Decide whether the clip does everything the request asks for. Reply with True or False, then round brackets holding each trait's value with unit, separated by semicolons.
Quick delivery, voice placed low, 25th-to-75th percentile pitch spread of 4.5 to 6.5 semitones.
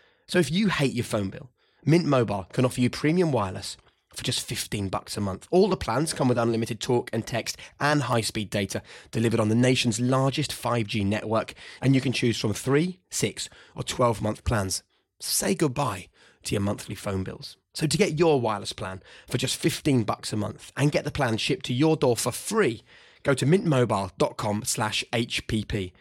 False (190 wpm; 120 Hz; 4.8 semitones)